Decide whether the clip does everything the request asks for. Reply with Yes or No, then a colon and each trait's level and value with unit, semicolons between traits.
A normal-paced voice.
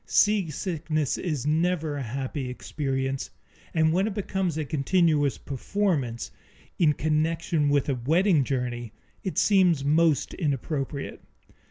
No: slow, 120 wpm